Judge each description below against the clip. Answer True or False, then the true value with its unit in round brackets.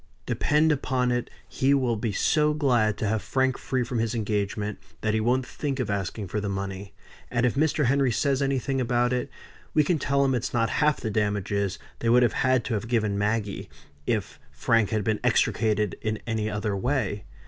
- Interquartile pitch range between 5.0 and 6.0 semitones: False (3.9 semitones)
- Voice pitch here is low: True (115 Hz)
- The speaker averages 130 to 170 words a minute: False (200 wpm)